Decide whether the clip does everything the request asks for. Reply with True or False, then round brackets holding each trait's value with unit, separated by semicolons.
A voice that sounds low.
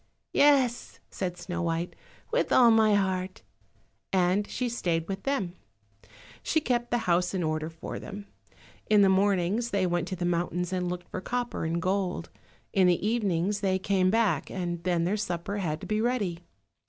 False (190 Hz)